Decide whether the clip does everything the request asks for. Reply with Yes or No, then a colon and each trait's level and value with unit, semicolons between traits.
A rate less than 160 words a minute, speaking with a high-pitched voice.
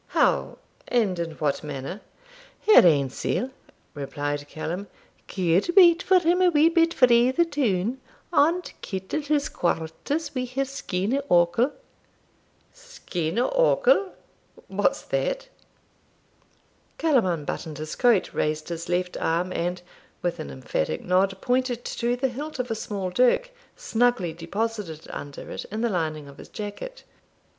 Yes: slow, 135 wpm; high, 215 Hz